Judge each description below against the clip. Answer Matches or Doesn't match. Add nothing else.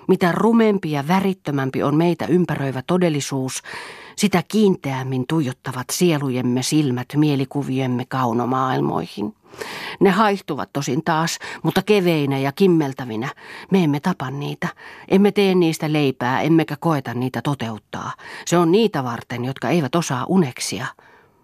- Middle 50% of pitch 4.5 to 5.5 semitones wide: Matches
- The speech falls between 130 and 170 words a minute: Doesn't match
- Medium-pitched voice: Matches